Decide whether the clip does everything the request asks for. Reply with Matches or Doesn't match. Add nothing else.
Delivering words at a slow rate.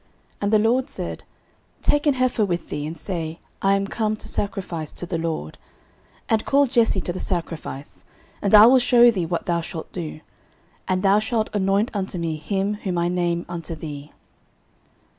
Doesn't match